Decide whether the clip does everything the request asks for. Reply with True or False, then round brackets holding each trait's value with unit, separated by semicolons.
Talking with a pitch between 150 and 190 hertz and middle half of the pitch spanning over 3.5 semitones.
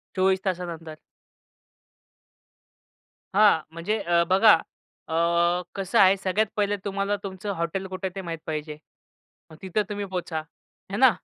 False (185 Hz; 2.7 semitones)